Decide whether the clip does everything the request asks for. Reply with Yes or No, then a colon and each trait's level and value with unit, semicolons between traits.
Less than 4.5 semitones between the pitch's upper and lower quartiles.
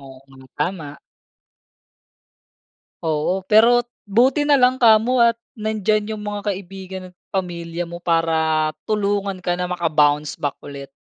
No: average, 5.1 semitones